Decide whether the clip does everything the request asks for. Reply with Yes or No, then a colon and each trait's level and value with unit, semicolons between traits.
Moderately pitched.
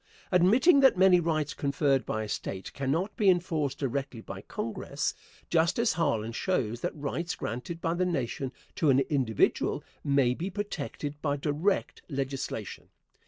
Yes: medium, 150 Hz